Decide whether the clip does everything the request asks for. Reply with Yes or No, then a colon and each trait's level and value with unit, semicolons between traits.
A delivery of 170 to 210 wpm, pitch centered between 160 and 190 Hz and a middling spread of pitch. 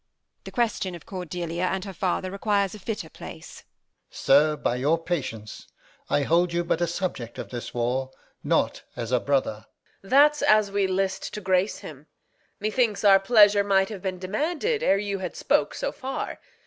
Yes: average, 180 wpm; medium, 185 Hz; average, 4.3 semitones